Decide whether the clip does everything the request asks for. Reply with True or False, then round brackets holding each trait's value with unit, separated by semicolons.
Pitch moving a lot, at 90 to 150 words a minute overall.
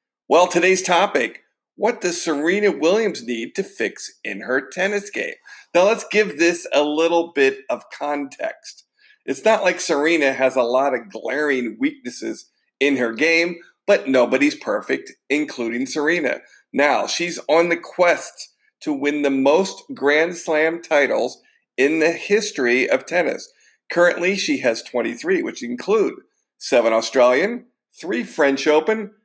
True (6.9 semitones; 140 wpm)